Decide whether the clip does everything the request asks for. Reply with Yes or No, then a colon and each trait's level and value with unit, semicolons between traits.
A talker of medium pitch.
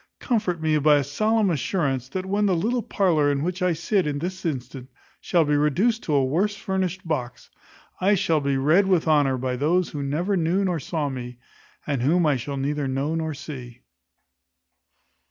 Yes: medium, 155 Hz